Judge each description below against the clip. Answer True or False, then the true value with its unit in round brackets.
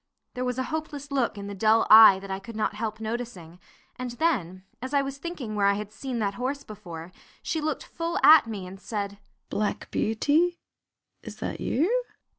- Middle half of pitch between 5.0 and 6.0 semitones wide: True (5.6 semitones)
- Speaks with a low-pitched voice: False (225 Hz)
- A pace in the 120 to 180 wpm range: False (195 wpm)